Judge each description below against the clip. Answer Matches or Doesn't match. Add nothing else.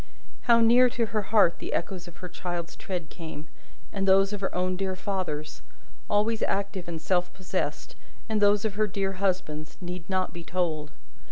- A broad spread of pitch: Doesn't match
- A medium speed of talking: Matches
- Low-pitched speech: Doesn't match